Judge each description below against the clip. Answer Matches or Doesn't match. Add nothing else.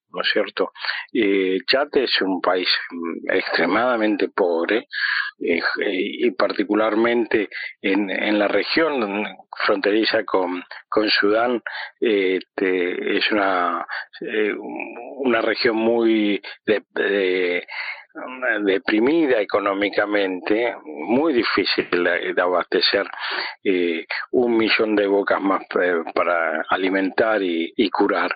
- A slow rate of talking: Matches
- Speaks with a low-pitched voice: Matches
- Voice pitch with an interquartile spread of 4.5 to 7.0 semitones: Doesn't match